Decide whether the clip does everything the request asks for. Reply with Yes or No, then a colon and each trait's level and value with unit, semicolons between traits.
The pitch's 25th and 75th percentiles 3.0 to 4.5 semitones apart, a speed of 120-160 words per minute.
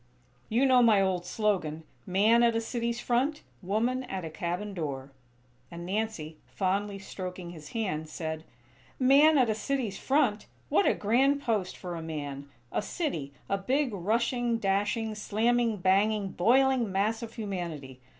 No: average, 5.0 semitones; average, 150 wpm